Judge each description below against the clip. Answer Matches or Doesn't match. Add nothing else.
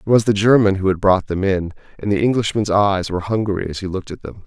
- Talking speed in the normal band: Doesn't match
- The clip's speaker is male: Matches